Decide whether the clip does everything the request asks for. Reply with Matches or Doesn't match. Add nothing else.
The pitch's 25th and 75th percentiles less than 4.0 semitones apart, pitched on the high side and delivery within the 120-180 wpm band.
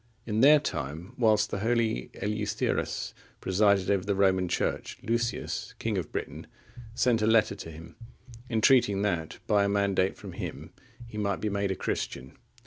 Doesn't match